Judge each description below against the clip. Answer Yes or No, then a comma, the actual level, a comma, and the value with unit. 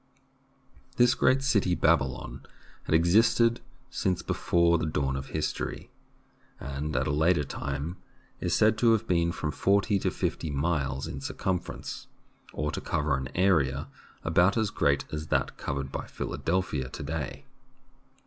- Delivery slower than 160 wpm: Yes, average, 150 wpm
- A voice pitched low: Yes, very low, 80 Hz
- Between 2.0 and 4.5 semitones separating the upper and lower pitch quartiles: No, average, 5.2 semitones